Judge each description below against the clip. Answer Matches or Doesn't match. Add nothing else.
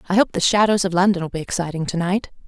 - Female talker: Matches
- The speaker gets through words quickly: Matches